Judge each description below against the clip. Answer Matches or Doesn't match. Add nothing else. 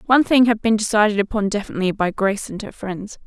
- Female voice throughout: Matches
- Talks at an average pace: Doesn't match